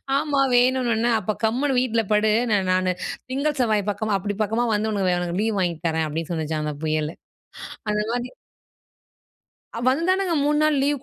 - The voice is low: No, high, 220 Hz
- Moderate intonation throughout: No, wide, 6.1 semitones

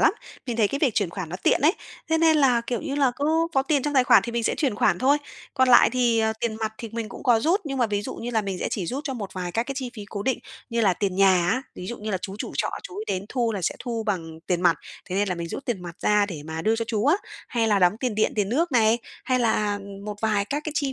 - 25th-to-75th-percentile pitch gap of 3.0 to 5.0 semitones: Yes, average, 4.7 semitones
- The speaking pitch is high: Yes, high, 225 Hz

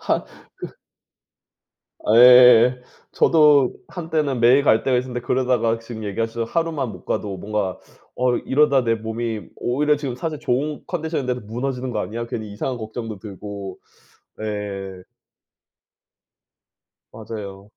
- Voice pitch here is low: Yes, low, 120 Hz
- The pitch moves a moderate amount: Yes, average, 3.5 semitones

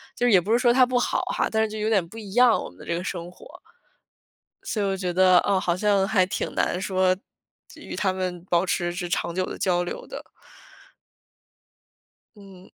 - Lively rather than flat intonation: No, average, 3.0 semitones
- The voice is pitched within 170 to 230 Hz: Yes, high, 190 Hz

